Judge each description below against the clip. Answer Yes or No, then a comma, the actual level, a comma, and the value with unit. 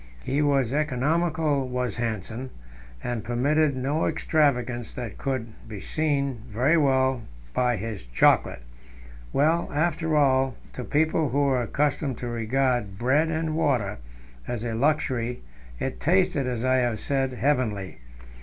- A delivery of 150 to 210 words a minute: No, slow, 135 wpm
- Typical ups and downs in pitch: Yes, average, 3.7 semitones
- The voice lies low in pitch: Yes, low, 130 Hz